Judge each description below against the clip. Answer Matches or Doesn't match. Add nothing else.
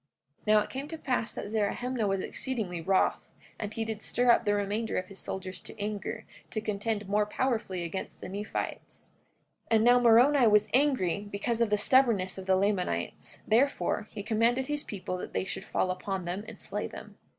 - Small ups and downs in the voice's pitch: Doesn't match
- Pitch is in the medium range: Doesn't match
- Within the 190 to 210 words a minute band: Matches